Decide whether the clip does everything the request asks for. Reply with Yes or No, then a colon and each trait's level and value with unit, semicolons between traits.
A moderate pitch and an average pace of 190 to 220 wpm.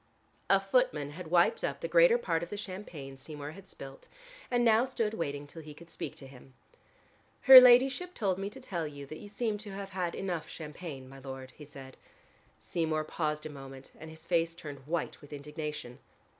Yes: medium, 160 Hz; average, 200 wpm